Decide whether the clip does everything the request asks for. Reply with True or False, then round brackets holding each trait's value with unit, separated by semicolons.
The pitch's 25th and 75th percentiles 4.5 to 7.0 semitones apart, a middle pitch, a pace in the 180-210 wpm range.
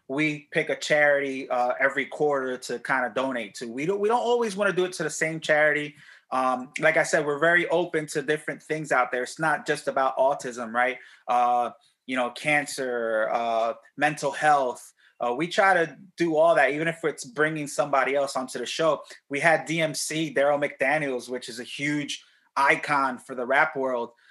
False (3.5 semitones; 145 Hz; 200 wpm)